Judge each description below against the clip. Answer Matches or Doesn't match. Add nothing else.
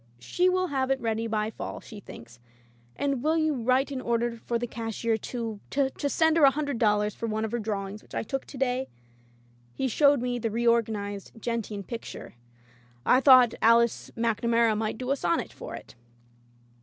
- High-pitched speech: Matches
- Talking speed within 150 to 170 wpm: Doesn't match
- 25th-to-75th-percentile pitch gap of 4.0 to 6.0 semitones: Doesn't match